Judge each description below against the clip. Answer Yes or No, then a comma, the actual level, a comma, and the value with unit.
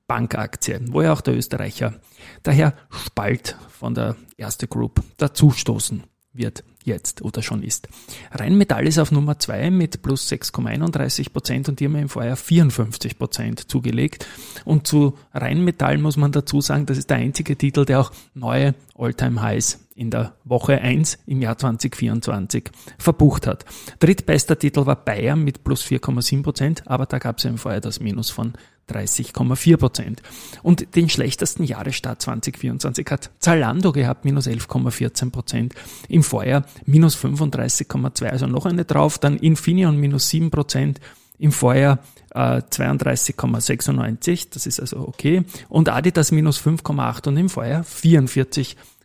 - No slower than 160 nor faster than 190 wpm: No, average, 145 wpm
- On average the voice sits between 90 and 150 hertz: Yes, low, 135 Hz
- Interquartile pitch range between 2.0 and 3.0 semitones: No, average, 3.7 semitones